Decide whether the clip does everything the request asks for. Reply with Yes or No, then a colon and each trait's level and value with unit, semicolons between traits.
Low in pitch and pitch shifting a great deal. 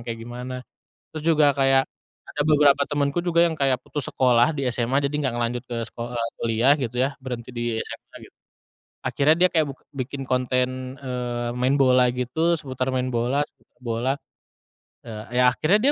No: low, 130 Hz; narrow, 2.5 semitones